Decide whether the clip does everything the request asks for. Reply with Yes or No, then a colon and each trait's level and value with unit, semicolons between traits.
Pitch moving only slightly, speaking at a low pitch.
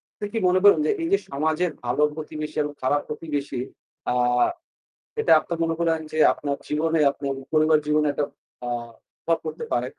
No: narrow, 2.0 semitones; medium, 155 Hz